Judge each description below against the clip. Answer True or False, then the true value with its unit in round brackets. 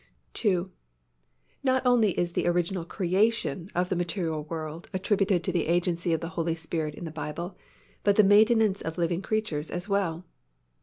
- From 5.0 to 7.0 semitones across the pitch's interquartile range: False (3.2 semitones)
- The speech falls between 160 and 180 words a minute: True (165 wpm)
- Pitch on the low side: False (175 Hz)